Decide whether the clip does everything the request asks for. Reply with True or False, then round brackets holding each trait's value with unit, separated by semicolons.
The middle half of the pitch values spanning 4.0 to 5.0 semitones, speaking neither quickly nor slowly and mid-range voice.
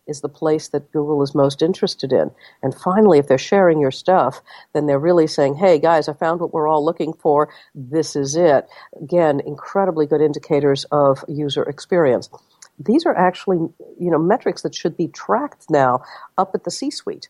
False (3.3 semitones; 190 wpm; 155 Hz)